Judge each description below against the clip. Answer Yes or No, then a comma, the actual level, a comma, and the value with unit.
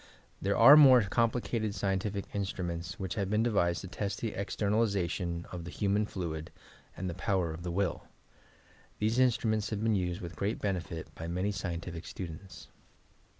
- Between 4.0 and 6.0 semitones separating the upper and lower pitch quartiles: No, average, 3.4 semitones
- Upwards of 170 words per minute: No, average, 165 wpm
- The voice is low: Yes, very low, 95 Hz